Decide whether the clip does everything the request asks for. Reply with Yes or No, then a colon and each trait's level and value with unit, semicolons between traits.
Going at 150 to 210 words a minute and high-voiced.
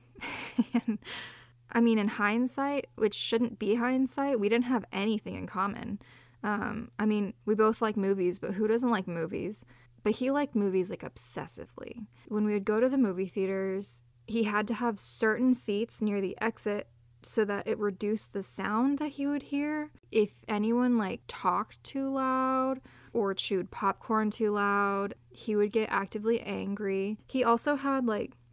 Yes: average, 170 wpm; high, 215 Hz